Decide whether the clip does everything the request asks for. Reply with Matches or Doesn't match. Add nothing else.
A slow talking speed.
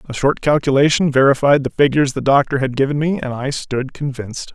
Doesn't match